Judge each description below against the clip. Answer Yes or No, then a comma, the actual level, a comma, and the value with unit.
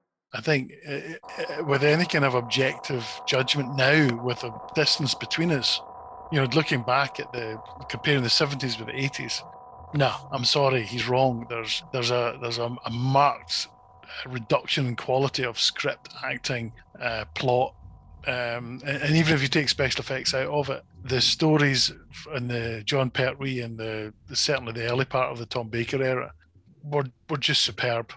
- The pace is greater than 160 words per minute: Yes, average, 175 wpm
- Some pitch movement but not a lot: Yes, average, 3.0 semitones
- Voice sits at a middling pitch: No, low, 130 Hz